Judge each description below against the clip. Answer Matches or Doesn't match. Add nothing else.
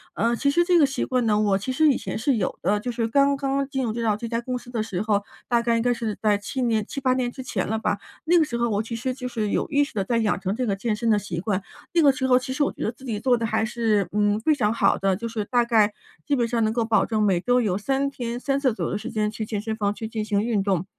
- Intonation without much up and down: Doesn't match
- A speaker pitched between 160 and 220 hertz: Doesn't match